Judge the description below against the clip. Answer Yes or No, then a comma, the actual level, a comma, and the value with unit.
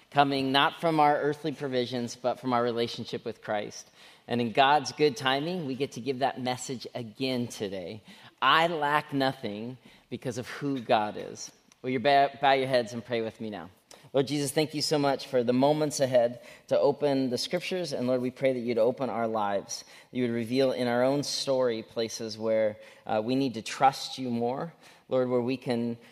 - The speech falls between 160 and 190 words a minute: No, average, 200 wpm